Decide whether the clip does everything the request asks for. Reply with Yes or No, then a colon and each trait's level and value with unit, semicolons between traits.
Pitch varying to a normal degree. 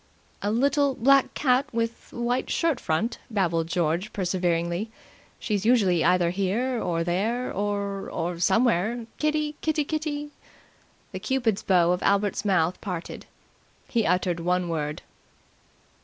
No: wide, 5.7 semitones